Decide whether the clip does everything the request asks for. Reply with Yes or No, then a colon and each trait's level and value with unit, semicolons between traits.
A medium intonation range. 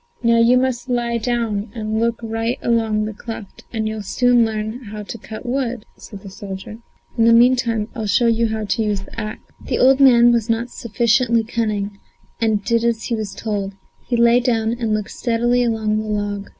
No: narrow, 1.8 semitones